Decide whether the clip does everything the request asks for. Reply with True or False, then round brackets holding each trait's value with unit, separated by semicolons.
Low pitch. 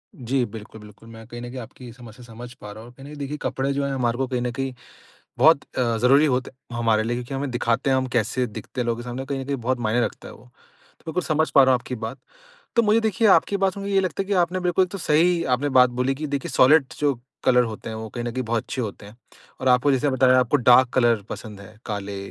True (125 Hz)